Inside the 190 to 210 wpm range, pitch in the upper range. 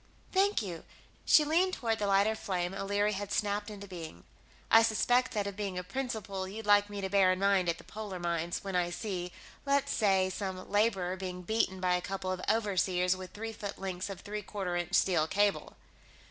Yes: average, 200 wpm; high, 195 Hz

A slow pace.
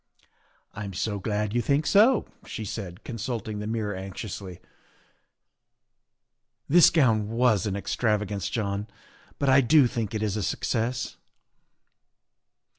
Yes: slow, 130 wpm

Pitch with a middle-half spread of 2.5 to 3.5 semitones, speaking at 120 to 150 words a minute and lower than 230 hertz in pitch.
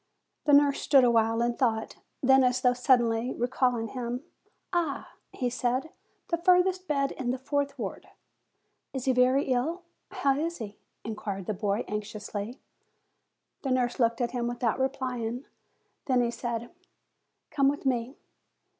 No: average, 2.8 semitones; average, 145 wpm; very high, 250 Hz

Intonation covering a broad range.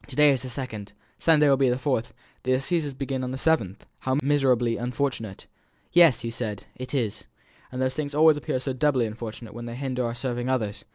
No: average, 2.9 semitones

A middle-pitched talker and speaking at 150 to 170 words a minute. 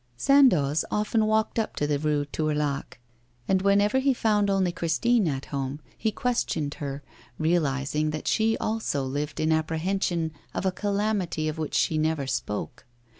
Yes: medium, 160 Hz; average, 155 wpm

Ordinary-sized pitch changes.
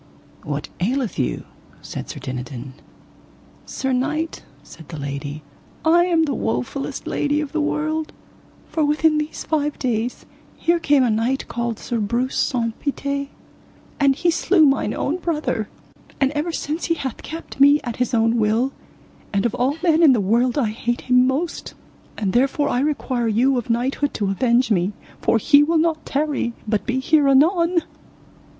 Yes: average, 4.9 semitones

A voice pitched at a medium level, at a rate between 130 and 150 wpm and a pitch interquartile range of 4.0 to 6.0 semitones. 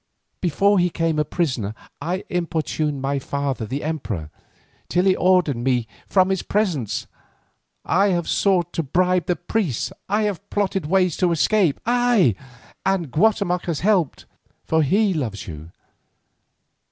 Yes: medium, 175 Hz; average, 140 wpm; average, 5.3 semitones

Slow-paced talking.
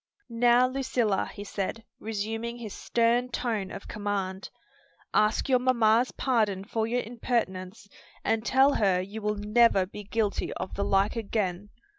No: average, 145 wpm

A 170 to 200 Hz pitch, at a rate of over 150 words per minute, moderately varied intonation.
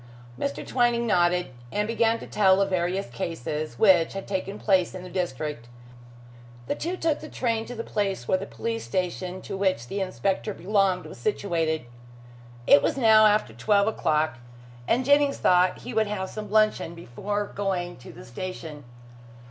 Yes: high, 190 Hz; average, 170 wpm; average, 3.8 semitones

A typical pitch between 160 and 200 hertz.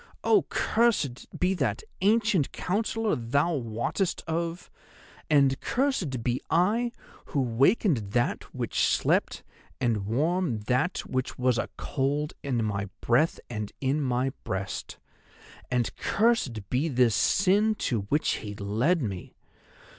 No: low, 135 Hz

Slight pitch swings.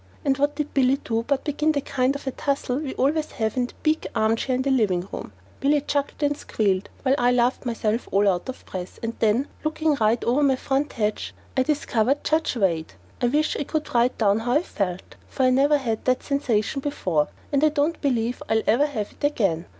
No: average, 4.5 semitones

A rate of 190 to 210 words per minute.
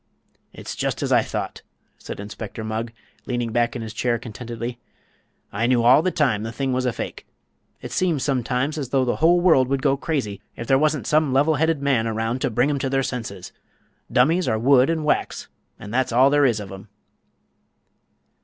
Yes: average, 200 wpm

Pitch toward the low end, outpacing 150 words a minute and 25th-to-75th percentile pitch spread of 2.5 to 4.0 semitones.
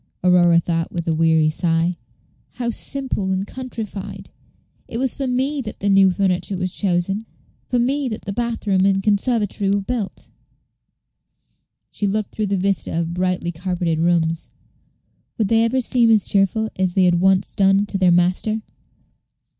No: high, 195 Hz; average, 160 wpm; average, 3.7 semitones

